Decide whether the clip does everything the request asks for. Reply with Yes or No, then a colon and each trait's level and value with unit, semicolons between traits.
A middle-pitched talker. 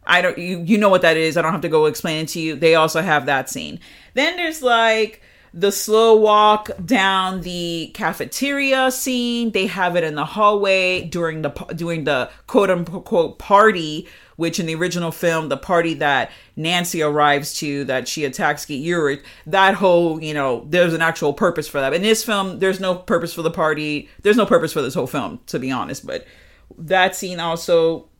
Yes: medium, 175 Hz